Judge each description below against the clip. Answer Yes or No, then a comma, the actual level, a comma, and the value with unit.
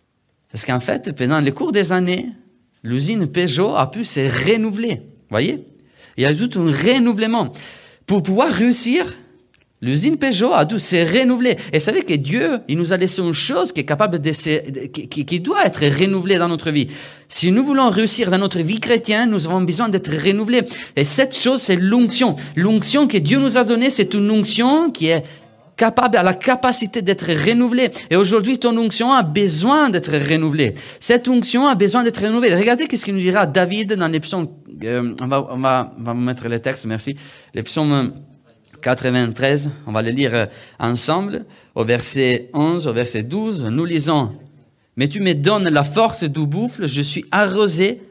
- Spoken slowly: No, average, 185 wpm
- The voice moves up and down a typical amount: No, wide, 7.8 semitones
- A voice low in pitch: No, medium, 180 Hz